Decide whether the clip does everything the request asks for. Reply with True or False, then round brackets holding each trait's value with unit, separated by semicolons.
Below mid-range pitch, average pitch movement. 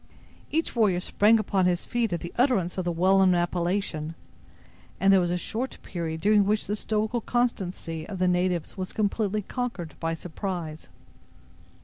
False (190 Hz; 3.5 semitones)